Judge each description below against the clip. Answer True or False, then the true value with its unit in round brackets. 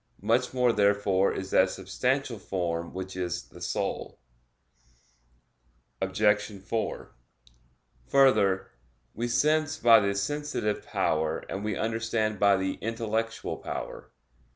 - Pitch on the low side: True (105 Hz)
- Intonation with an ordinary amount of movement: True (3.3 semitones)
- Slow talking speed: True (110 wpm)